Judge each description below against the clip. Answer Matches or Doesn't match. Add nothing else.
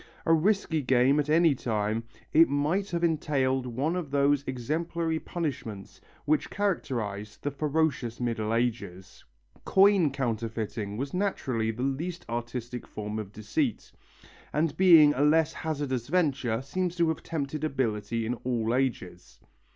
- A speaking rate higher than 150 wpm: Doesn't match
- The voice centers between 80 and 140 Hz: Matches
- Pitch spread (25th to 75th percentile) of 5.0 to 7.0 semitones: Matches